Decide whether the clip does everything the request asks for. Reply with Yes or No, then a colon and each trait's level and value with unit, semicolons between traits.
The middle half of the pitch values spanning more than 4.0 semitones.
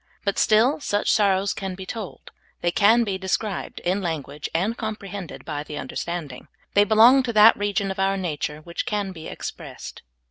No: average, 3.6 semitones